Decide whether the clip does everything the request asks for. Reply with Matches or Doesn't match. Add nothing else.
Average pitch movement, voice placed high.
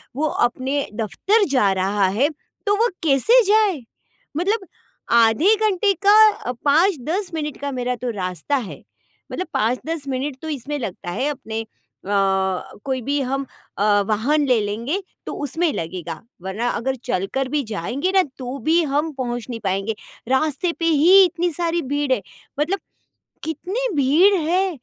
Doesn't match